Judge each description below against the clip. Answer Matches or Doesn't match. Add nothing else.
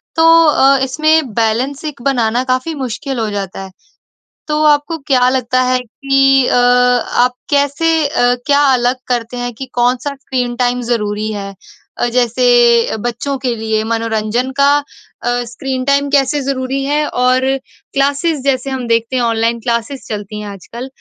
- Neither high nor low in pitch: Doesn't match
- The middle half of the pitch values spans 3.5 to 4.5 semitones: Doesn't match